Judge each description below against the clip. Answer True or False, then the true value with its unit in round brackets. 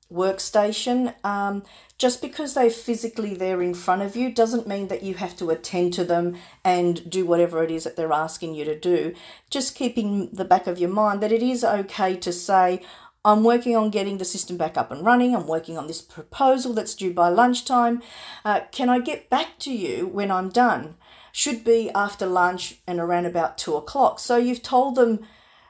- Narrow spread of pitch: False (5.2 semitones)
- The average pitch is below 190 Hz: False (200 Hz)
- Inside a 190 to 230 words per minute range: True (200 wpm)